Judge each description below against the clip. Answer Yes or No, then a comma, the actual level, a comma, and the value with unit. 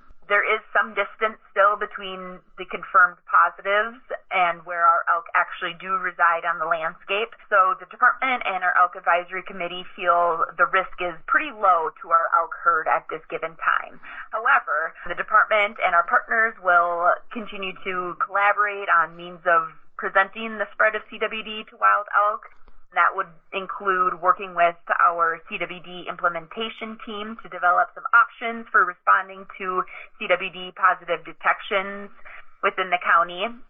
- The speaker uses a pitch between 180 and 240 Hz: Yes, medium, 185 Hz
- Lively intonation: No, average, 3.1 semitones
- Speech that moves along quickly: No, average, 150 wpm